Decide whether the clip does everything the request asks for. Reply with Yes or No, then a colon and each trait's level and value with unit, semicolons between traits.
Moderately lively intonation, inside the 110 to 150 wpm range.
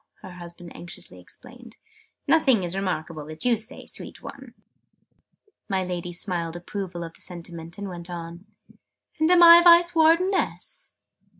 No: wide, 6.5 semitones; average, 140 wpm